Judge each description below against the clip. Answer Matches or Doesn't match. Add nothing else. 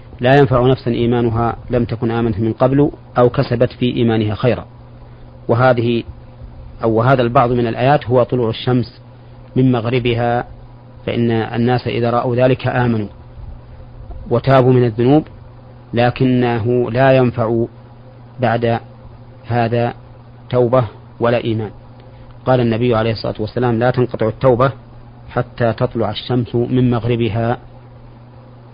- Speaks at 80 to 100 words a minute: Doesn't match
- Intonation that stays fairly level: Matches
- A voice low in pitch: Matches